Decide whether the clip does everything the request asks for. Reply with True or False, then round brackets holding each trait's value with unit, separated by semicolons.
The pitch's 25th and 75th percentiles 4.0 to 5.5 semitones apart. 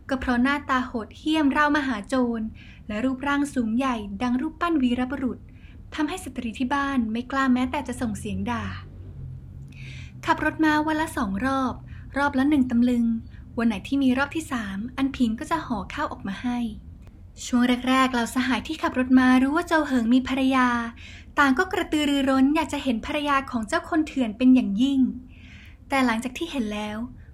False (2.9 semitones)